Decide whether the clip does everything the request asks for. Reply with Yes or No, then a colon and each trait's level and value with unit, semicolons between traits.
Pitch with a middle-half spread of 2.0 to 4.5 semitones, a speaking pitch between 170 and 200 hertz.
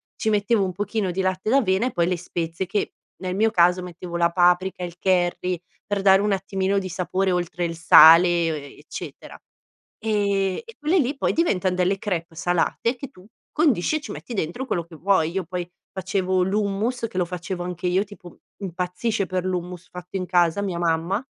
Yes: narrow, 2.4 semitones; medium, 185 Hz